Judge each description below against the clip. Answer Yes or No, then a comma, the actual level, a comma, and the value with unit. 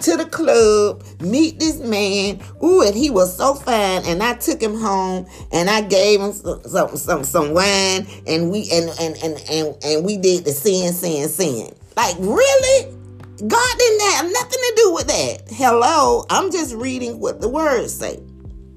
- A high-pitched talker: Yes, high, 210 Hz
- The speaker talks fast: No, average, 180 wpm